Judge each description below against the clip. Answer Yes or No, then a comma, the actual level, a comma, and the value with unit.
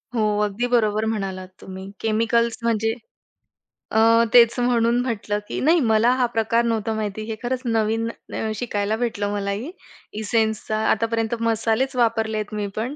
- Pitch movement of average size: No, narrow, 1.7 semitones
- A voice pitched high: Yes, high, 225 Hz